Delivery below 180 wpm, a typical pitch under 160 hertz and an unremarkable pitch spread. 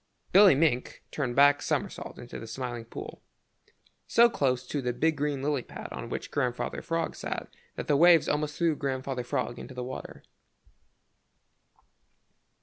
Yes: average, 155 wpm; medium, 140 Hz; average, 3.4 semitones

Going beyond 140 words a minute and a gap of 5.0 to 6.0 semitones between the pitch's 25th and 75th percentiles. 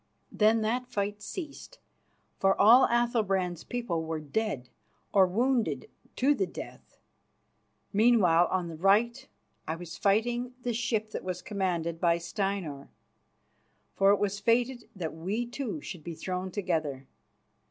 No: slow, 135 wpm; wide, 5.4 semitones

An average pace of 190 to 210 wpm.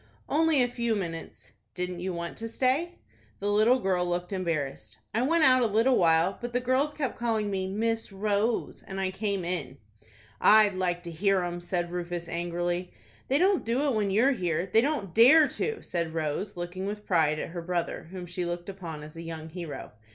Yes: fast, 205 wpm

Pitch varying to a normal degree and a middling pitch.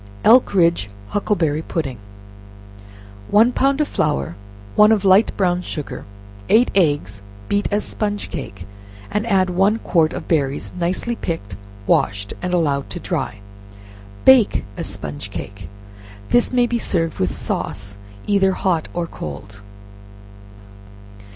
No: wide, 7.3 semitones; medium, 175 Hz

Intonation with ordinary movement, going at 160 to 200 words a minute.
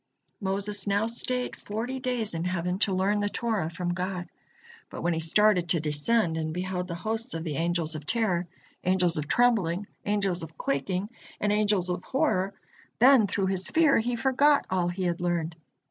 Yes: average, 3.9 semitones; average, 180 wpm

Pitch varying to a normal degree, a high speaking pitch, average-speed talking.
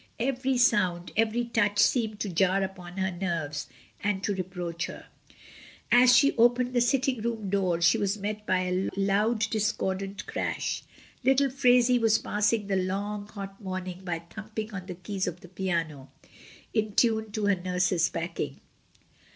Yes: average, 3.5 semitones; high, 200 Hz; average, 160 wpm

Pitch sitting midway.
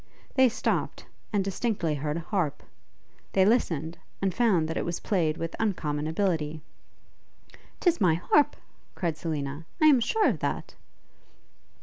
Yes: medium, 175 Hz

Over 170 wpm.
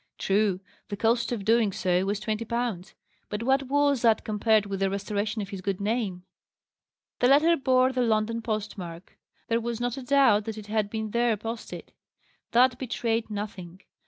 Yes: average, 180 wpm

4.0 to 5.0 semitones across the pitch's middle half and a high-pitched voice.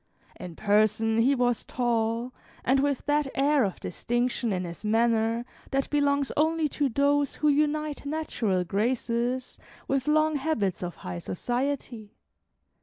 Yes: average, 4.4 semitones; high, 245 Hz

